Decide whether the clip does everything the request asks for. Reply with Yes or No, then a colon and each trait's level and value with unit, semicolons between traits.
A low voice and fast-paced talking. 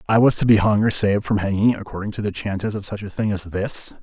Yes: low, 105 Hz; fast, 285 wpm